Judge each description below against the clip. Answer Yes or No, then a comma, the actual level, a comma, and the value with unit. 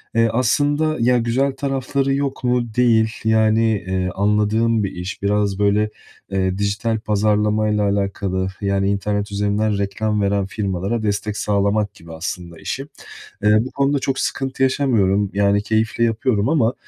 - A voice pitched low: Yes, low, 105 Hz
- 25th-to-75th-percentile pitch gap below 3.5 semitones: Yes, average, 2.8 semitones